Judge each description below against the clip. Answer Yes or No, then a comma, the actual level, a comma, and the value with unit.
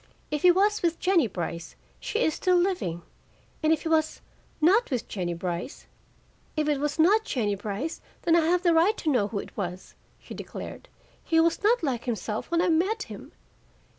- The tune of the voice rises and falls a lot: Yes, wide, 8.8 semitones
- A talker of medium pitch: No, very high, 315 Hz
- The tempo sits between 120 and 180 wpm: No, average, 195 wpm